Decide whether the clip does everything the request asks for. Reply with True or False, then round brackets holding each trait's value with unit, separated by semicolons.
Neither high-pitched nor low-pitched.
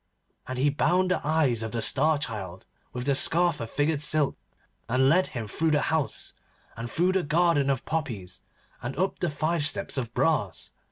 True (145 Hz)